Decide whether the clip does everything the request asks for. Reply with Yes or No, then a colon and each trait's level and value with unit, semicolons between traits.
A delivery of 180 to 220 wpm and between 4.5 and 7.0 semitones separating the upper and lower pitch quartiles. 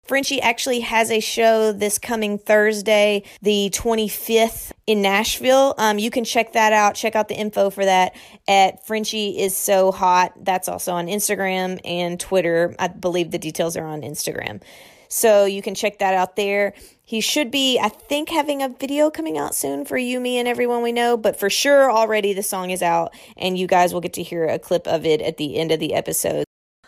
No: fast, 205 wpm; average, 3.7 semitones